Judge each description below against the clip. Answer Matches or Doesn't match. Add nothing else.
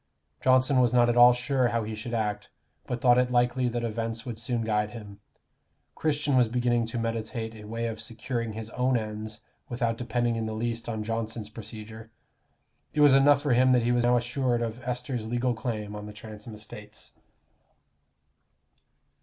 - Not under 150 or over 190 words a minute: Matches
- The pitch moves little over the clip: Matches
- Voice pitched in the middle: Doesn't match